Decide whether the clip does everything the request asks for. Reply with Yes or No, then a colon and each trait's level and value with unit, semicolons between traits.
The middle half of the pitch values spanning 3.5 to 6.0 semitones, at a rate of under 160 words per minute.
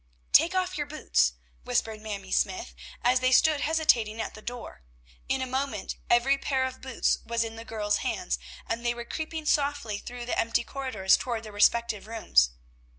No: average, 4.1 semitones; average, 180 wpm